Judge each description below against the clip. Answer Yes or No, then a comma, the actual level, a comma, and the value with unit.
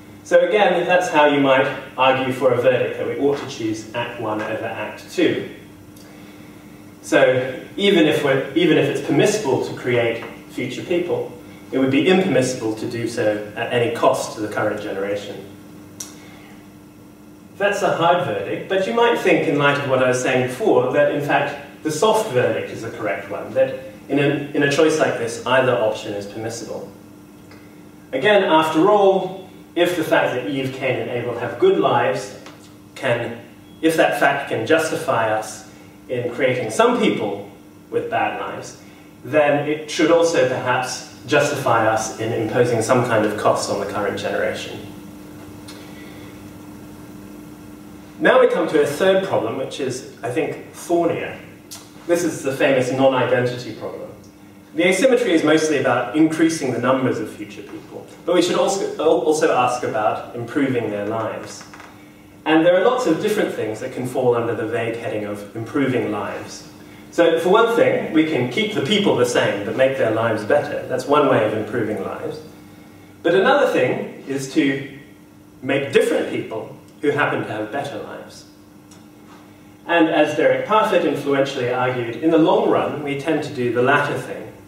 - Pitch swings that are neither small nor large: No, wide, 7.5 semitones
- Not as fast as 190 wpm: Yes, average, 170 wpm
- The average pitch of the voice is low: Yes, low, 130 Hz